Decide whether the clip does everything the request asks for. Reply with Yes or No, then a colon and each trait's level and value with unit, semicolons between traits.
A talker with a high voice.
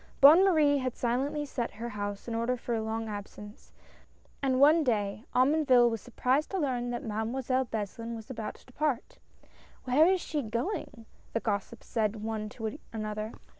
Yes: high, 240 Hz